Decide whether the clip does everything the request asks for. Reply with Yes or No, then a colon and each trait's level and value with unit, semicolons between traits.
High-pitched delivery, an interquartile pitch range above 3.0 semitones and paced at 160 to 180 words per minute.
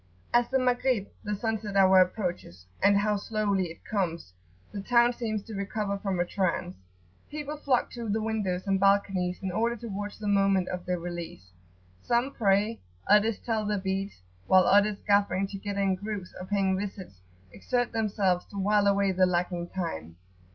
No: high, 200 Hz; narrow, 2.4 semitones; average, 170 wpm